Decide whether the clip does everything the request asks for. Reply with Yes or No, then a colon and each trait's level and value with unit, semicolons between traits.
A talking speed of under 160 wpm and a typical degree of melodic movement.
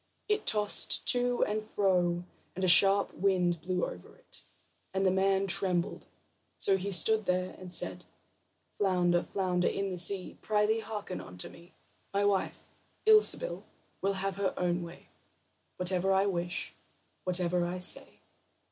No: average, 145 wpm; narrow, 2.1 semitones